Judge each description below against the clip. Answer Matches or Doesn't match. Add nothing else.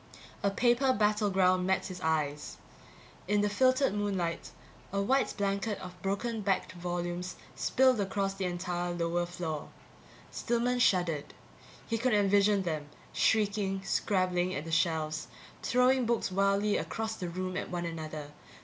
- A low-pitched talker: Doesn't match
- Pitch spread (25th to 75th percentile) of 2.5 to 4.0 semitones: Matches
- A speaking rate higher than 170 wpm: Doesn't match